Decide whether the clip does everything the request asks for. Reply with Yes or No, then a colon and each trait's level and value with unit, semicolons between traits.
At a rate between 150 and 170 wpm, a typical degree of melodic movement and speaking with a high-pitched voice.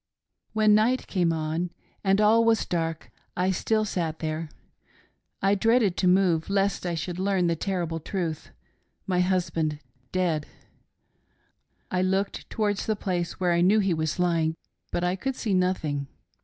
No: average, 160 wpm; average, 3.2 semitones; medium, 180 Hz